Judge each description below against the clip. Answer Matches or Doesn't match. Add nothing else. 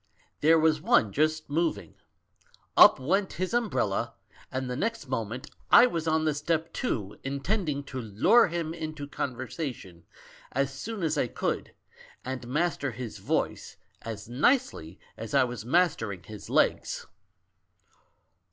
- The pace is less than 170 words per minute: Matches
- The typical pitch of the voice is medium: Matches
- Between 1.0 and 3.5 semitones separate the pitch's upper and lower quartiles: Doesn't match